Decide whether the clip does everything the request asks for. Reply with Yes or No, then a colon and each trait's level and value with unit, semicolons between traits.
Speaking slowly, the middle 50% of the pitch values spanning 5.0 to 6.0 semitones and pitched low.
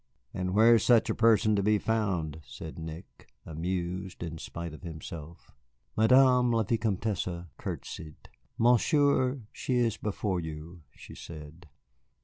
Yes: slow, 130 wpm; wide, 5.4 semitones; very low, 95 Hz